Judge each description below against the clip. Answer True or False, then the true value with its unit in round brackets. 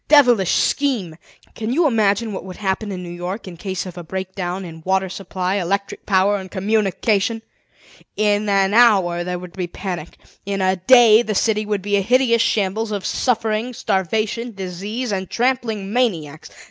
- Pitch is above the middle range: True (200 Hz)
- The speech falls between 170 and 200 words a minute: True (175 wpm)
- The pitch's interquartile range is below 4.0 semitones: True (3.0 semitones)